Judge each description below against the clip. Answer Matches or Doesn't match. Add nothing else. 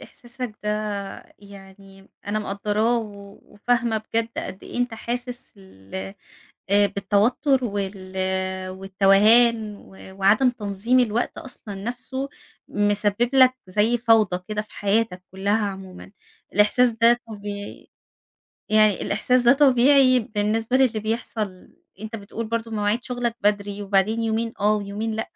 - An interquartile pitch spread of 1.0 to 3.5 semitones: Matches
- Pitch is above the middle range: Matches